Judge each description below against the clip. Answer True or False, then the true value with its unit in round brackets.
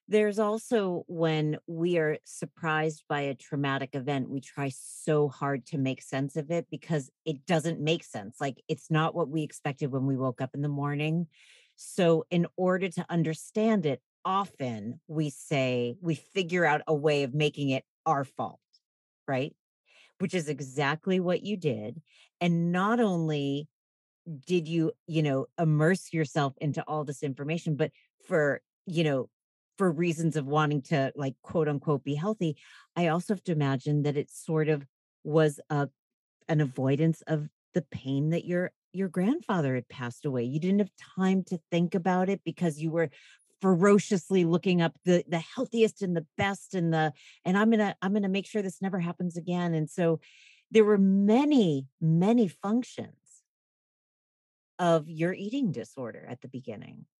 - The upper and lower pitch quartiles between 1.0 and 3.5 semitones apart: False (4.0 semitones)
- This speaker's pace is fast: False (170 wpm)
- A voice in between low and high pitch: True (160 Hz)